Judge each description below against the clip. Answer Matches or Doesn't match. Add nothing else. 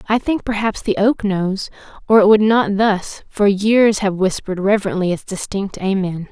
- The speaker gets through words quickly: Doesn't match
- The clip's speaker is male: Doesn't match